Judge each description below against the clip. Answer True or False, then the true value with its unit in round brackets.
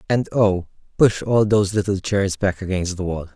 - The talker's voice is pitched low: True (100 Hz)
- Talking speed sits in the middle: True (195 wpm)